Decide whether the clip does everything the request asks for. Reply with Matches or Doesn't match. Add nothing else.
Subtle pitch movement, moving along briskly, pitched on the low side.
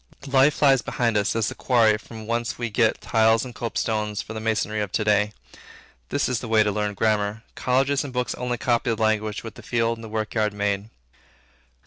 Matches